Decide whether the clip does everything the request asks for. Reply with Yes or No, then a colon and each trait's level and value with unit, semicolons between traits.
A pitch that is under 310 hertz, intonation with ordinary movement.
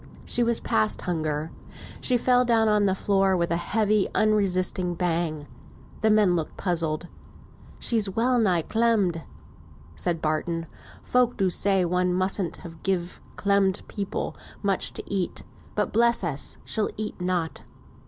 Yes: high, 190 Hz; average, 3.8 semitones